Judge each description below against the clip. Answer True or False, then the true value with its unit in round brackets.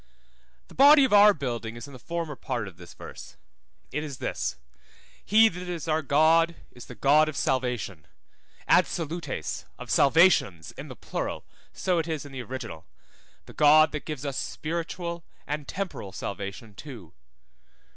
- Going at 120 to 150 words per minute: False (165 wpm)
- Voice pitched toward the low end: False (150 Hz)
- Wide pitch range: True (5.8 semitones)